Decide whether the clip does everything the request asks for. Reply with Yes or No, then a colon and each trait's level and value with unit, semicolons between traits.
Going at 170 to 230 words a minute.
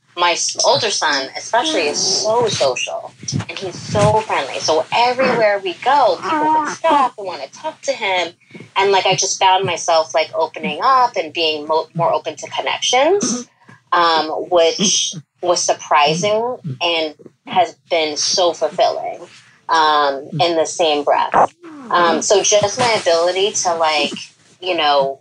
No: average, 150 wpm